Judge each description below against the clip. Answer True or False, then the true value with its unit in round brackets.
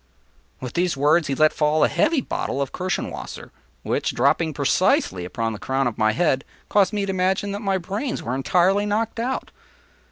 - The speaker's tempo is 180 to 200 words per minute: True (190 wpm)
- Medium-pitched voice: True (175 Hz)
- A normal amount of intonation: False (7.0 semitones)